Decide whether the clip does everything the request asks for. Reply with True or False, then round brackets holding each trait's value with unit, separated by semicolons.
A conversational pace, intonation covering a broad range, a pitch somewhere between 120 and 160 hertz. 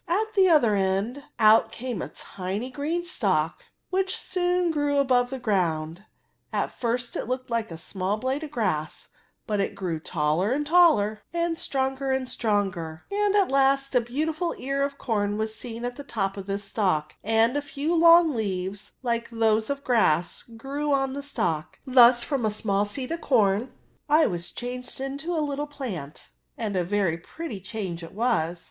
False (180 wpm; 6.0 semitones; 240 Hz)